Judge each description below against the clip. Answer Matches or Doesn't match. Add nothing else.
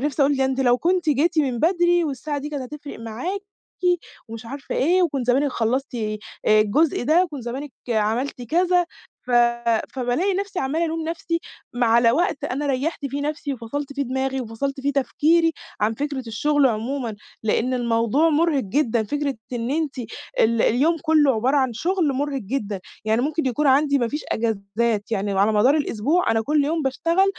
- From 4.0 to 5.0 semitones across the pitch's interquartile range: Matches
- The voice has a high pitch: Matches